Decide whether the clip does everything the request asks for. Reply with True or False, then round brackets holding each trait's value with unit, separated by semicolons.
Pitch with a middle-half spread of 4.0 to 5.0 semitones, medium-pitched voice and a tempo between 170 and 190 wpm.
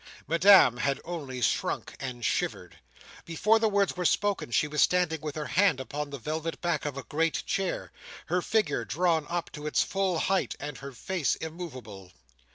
True (4.5 semitones; 160 Hz; 175 wpm)